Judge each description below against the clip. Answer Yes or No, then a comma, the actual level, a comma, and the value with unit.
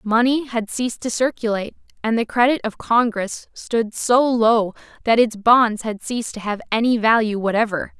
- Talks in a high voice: Yes, high, 230 Hz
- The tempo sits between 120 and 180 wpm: Yes, average, 175 wpm